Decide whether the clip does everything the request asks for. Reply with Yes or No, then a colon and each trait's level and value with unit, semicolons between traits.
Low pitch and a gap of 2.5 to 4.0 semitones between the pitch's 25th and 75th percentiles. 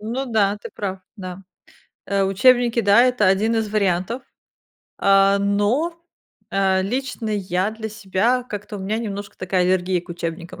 No: high, 200 Hz; average, 2.9 semitones